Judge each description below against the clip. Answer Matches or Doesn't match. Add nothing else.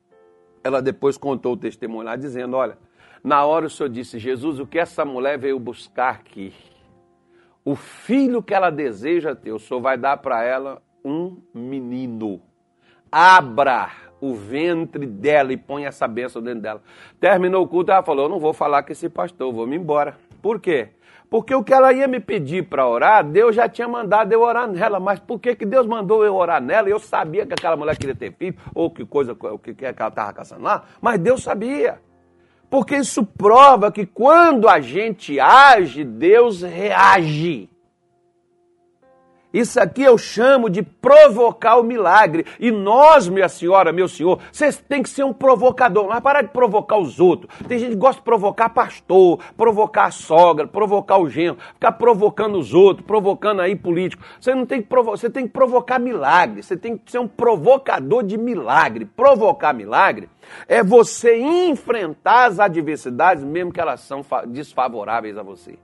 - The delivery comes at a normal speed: Matches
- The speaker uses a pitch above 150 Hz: Matches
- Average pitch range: Doesn't match